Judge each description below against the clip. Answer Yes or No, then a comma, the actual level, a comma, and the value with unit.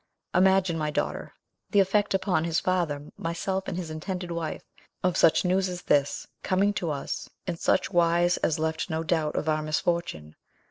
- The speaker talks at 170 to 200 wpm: Yes, average, 175 wpm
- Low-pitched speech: No, medium, 170 Hz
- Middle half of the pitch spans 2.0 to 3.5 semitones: Yes, average, 2.8 semitones